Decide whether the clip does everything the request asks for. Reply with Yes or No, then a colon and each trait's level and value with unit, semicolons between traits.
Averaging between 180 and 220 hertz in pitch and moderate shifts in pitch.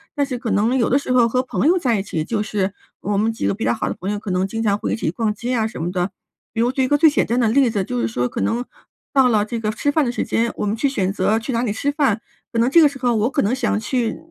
No: high, 230 Hz; average, 3.7 semitones